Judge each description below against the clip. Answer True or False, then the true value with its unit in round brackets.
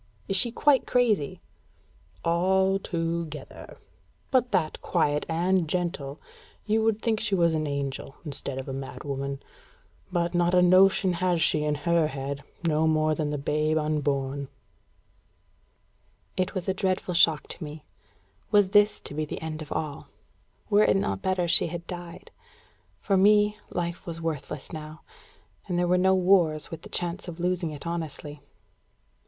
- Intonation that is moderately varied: True (3.6 semitones)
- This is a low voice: False (170 Hz)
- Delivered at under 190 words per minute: True (160 wpm)